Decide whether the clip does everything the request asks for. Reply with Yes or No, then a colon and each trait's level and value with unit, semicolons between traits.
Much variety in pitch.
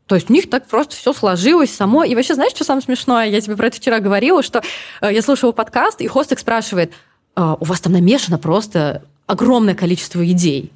Yes: wide, 5.9 semitones